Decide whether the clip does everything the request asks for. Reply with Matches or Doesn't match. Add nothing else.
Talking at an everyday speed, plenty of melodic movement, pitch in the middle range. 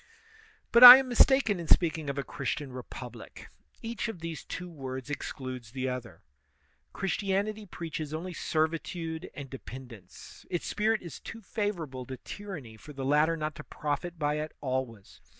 Matches